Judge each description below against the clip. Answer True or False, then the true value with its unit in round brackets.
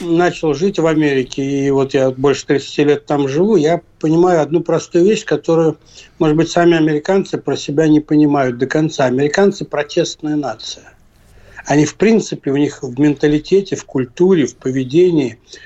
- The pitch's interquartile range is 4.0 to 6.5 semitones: False (3.1 semitones)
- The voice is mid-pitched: True (150 Hz)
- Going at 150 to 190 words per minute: True (160 wpm)